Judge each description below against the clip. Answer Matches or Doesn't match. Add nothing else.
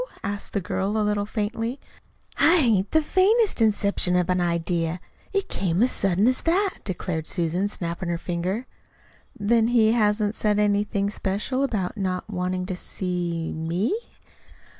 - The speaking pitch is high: Matches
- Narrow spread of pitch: Doesn't match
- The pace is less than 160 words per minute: Matches